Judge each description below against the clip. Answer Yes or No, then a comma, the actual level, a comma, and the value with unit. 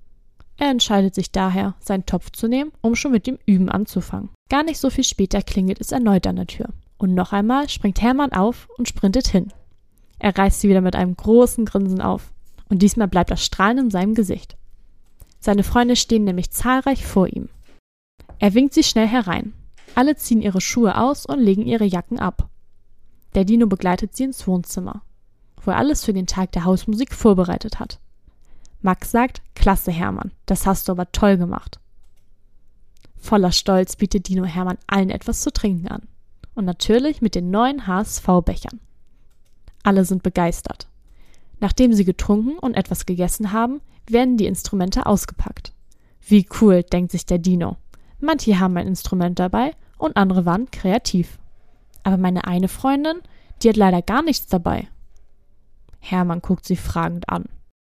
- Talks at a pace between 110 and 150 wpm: No, average, 165 wpm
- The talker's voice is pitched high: Yes, high, 195 Hz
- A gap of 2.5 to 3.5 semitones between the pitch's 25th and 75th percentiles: No, average, 4.2 semitones